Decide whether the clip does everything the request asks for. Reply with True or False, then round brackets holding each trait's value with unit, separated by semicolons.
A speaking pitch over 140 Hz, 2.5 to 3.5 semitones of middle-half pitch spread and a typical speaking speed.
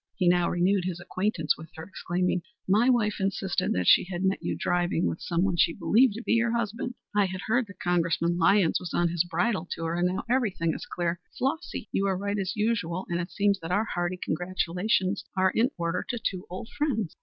False (185 Hz; 3.2 semitones; 215 wpm)